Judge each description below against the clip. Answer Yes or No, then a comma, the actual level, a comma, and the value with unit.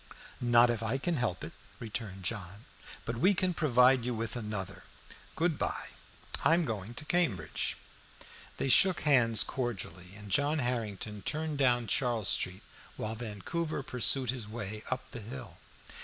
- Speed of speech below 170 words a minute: Yes, average, 155 wpm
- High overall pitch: No, low, 120 Hz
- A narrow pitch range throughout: No, average, 4.4 semitones